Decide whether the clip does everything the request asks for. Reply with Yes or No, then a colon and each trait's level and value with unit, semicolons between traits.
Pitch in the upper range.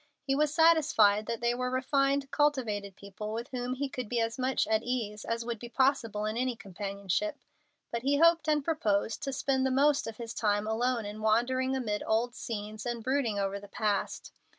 Yes: high, 240 Hz